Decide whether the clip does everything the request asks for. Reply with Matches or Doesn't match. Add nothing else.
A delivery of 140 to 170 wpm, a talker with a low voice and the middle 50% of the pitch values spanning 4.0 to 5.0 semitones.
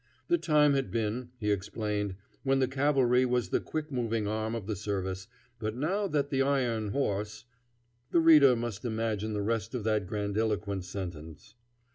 Matches